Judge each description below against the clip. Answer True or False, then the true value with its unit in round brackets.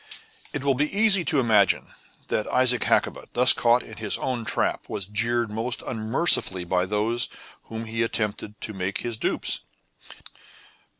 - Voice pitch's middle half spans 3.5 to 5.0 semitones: False (3.1 semitones)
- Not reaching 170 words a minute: True (155 wpm)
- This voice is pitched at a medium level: False (115 Hz)